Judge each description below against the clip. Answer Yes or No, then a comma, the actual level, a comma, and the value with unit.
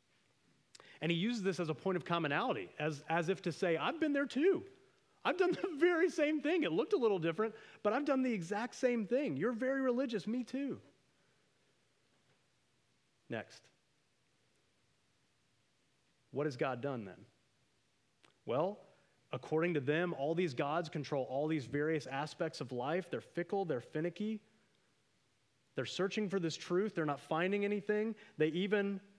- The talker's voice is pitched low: No, high, 190 Hz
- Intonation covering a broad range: Yes, wide, 7.4 semitones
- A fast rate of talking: No, average, 155 wpm